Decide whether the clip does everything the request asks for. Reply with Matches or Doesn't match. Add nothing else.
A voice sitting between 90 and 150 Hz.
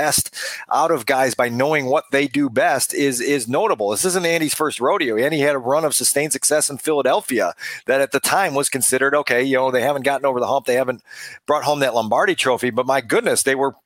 Matches